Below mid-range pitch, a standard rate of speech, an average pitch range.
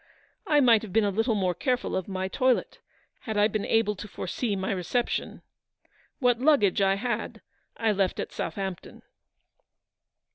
No: high, 210 Hz; average, 155 wpm; average, 3.9 semitones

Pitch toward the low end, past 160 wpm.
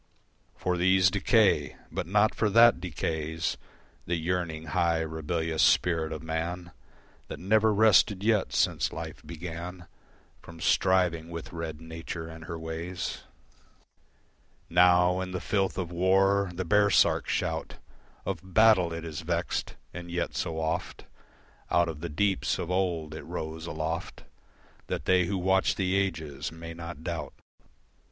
No: very low, 85 Hz; average, 140 wpm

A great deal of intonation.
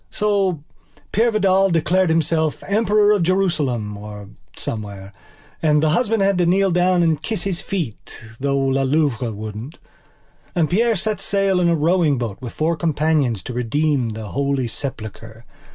Yes: wide, 7.3 semitones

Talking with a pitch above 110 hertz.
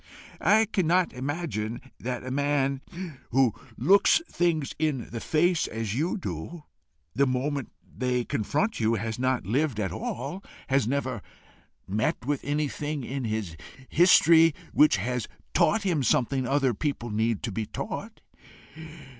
Yes: low, 135 Hz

